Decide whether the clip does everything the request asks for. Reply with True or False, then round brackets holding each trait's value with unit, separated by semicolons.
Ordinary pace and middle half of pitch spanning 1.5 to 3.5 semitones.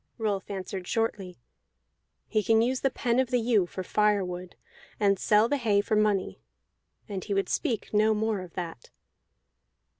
True (160 wpm; 2.7 semitones)